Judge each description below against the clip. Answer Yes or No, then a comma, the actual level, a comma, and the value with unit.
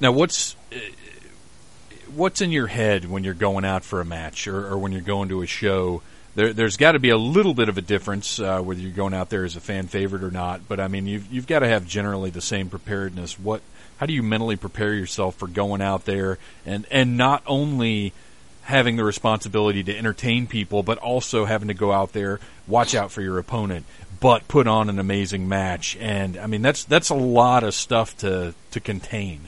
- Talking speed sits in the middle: No, fast, 215 wpm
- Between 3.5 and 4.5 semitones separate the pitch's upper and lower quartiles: No, average, 3.0 semitones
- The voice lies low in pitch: Yes, low, 100 Hz